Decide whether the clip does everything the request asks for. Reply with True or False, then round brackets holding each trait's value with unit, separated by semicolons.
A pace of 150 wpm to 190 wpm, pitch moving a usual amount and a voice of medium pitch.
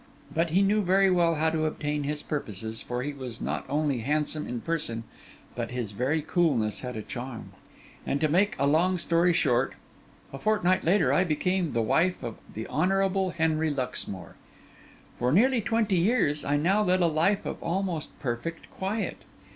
False (175 wpm; 5.7 semitones; 160 Hz)